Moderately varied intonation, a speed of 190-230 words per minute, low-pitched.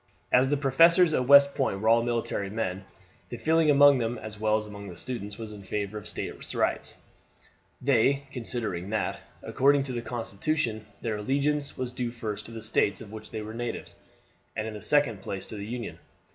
Yes: average, 4.2 semitones; average, 200 wpm; low, 115 Hz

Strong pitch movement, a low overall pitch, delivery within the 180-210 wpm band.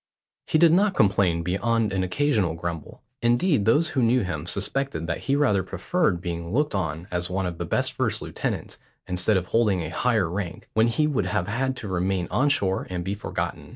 Yes: wide, 6.0 semitones; low, 100 Hz; average, 200 wpm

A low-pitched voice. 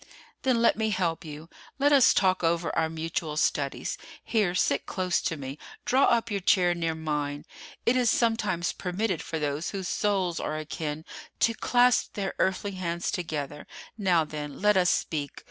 No: medium, 175 Hz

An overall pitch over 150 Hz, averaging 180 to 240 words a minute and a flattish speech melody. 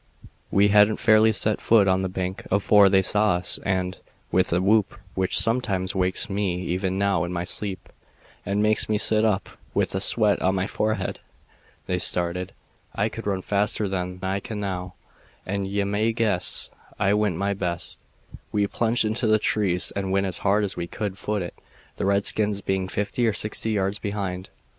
No: low, 100 Hz; average, 185 wpm; narrow, 2.2 semitones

